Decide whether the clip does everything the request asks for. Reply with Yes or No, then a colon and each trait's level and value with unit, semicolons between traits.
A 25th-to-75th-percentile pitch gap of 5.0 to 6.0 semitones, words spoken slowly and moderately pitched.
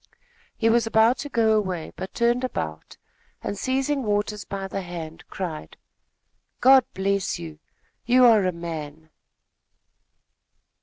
No: wide, 5.5 semitones; slow, 130 wpm; high, 200 Hz